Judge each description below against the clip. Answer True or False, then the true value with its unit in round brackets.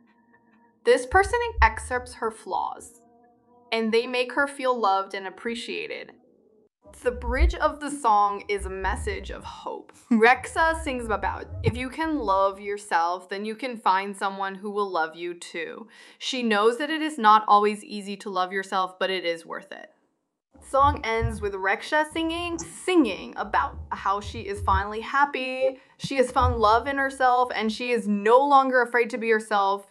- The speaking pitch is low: False (235 Hz)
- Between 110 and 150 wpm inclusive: False (170 wpm)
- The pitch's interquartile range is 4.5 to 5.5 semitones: True (5.2 semitones)